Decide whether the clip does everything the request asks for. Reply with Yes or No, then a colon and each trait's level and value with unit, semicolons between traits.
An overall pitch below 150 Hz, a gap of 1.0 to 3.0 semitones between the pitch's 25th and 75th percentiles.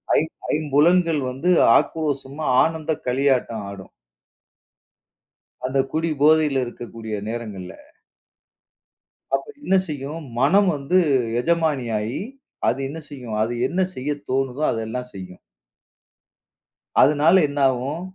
No: medium, 140 Hz; average, 4.0 semitones